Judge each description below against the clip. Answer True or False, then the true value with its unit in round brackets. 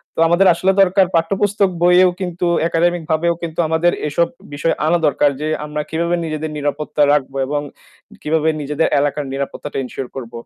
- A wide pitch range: False (2.9 semitones)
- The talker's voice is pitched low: False (160 Hz)